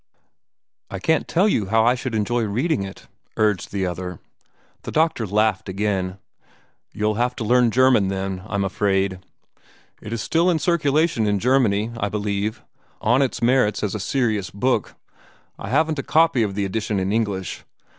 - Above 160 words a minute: Yes, average, 170 wpm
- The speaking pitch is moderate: No, low, 110 Hz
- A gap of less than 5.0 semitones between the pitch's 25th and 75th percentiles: Yes, average, 4.2 semitones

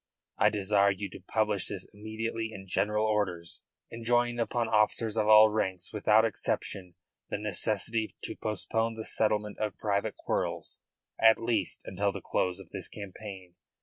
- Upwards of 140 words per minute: Yes, average, 150 wpm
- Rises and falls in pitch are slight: Yes, narrow, 2.1 semitones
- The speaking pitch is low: Yes, low, 105 Hz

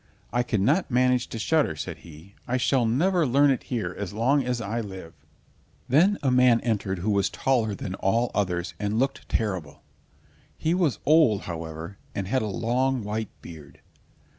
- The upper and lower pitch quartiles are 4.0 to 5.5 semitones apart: Yes, average, 5.1 semitones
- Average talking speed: Yes, average, 170 wpm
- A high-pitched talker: No, low, 115 Hz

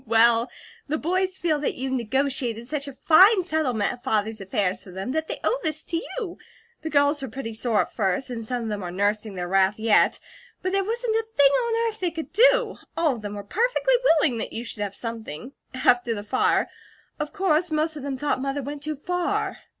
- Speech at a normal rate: No, fast, 220 wpm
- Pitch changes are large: Yes, wide, 6.8 semitones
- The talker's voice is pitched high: Yes, very high, 275 Hz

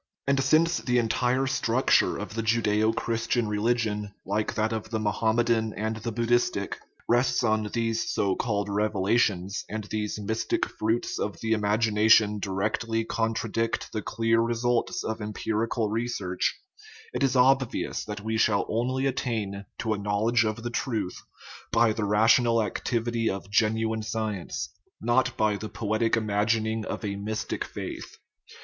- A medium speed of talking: Yes, average, 150 wpm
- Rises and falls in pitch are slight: Yes, narrow, 1.9 semitones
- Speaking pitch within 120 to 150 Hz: No, low, 110 Hz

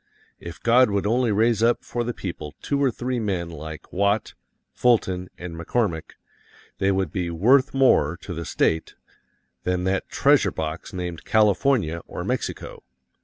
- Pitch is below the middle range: Yes, very low, 95 Hz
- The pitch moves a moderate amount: No, wide, 5.7 semitones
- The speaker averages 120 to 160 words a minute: Yes, average, 155 wpm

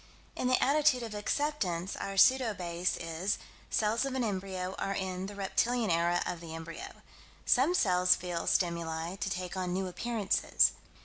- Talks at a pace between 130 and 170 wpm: Yes, average, 165 wpm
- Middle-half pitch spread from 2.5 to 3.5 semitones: No, average, 4.6 semitones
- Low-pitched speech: No, high, 190 Hz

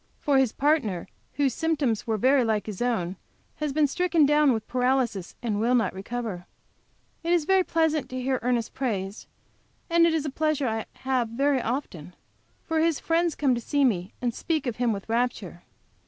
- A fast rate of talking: No, average, 185 wpm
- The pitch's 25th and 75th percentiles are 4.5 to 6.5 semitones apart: Yes, average, 5.0 semitones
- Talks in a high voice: Yes, very high, 255 Hz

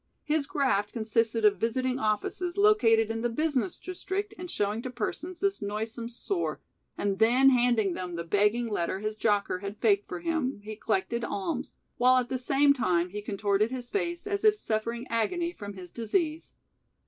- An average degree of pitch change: No, wide, 6.5 semitones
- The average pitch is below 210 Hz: No, high, 235 Hz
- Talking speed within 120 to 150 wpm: No, average, 175 wpm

